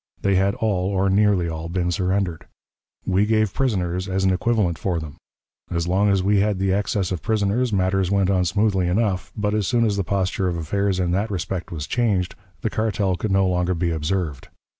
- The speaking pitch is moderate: No, very low, 95 Hz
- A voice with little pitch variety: Yes, narrow, 2.3 semitones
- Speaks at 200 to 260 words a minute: Yes, fast, 205 wpm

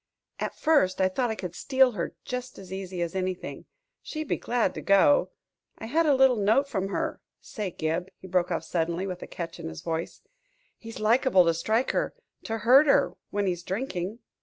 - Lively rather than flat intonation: Yes, wide, 5.7 semitones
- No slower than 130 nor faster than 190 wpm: No, average, 200 wpm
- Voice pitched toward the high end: Yes, high, 195 Hz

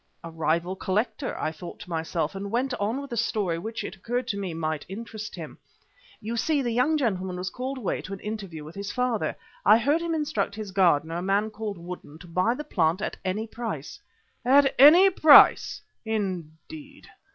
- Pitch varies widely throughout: Yes, wide, 5.7 semitones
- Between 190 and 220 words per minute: Yes, average, 195 wpm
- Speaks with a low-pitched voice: No, high, 210 Hz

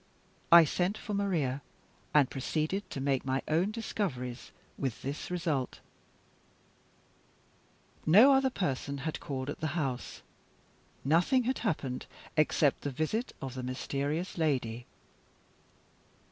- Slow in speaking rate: Yes, slow, 120 wpm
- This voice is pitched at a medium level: Yes, medium, 150 Hz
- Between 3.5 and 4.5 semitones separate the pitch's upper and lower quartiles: No, average, 5.3 semitones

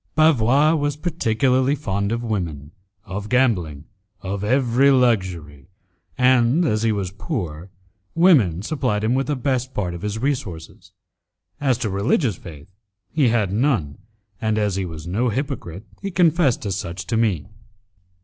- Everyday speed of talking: Yes, average, 150 wpm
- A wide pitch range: Yes, wide, 6.1 semitones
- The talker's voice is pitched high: No, low, 110 Hz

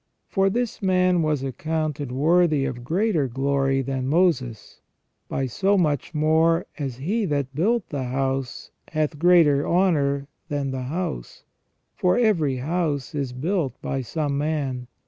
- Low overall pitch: No, medium, 145 Hz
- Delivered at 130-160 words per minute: Yes, average, 140 wpm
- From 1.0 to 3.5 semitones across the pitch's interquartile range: No, average, 4.4 semitones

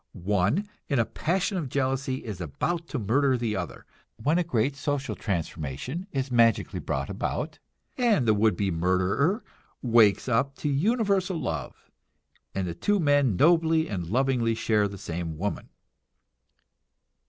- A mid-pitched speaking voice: No, low, 125 Hz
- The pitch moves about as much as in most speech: No, wide, 7.7 semitones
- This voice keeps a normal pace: Yes, average, 145 wpm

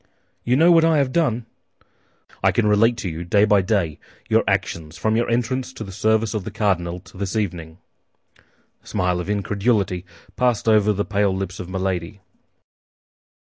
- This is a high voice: No, low, 105 Hz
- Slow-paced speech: No, average, 175 wpm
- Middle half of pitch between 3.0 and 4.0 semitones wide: Yes, average, 3.6 semitones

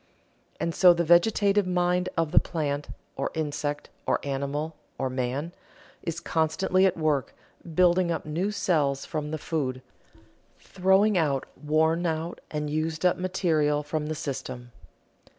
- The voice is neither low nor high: Yes, medium, 160 Hz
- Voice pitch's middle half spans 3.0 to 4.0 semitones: Yes, average, 3.3 semitones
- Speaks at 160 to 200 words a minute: No, average, 140 wpm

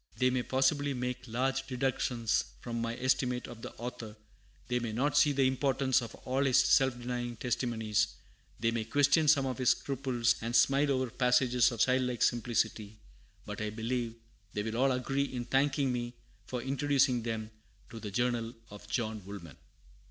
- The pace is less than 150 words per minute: No, average, 170 wpm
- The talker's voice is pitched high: No, low, 125 Hz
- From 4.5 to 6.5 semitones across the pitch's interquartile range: No, narrow, 2.4 semitones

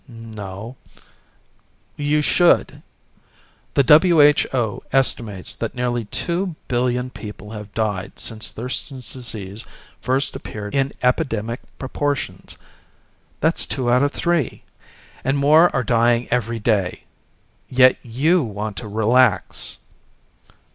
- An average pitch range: Yes, average, 4.2 semitones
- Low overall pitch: Yes, low, 125 Hz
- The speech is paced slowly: Yes, slow, 110 wpm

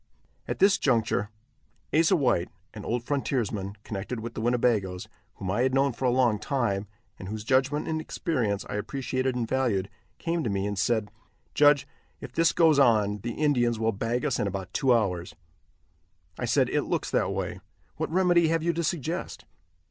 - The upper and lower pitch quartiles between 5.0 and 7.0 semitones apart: Yes, wide, 5.6 semitones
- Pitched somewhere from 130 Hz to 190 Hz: No, low, 120 Hz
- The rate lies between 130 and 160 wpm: No, average, 180 wpm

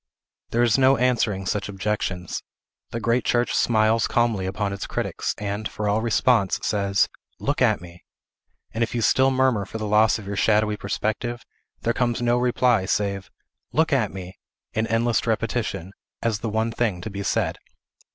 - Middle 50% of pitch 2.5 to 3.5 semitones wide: Yes, average, 2.9 semitones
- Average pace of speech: Yes, average, 170 wpm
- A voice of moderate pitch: No, low, 110 Hz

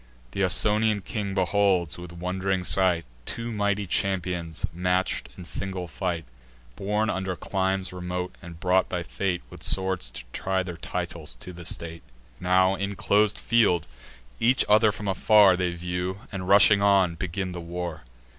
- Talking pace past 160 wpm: No, average, 155 wpm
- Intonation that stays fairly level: Yes, narrow, 2.0 semitones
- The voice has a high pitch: No, very low, 95 Hz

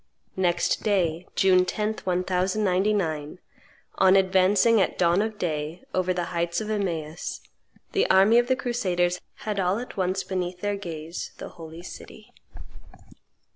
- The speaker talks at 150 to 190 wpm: No, slow, 135 wpm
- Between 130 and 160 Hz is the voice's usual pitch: No, medium, 185 Hz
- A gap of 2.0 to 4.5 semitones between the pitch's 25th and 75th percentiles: Yes, average, 2.8 semitones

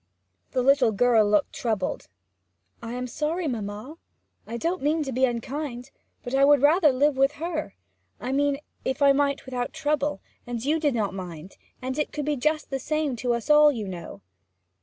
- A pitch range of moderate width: Yes, average, 4.0 semitones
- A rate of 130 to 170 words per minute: No, average, 185 wpm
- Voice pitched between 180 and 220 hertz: No, very high, 270 Hz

